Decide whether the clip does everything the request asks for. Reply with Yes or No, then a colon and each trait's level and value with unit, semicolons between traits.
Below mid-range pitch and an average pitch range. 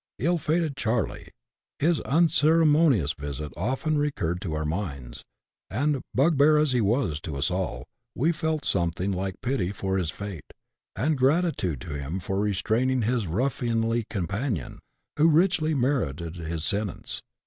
No: low, 115 Hz; wide, 9.0 semitones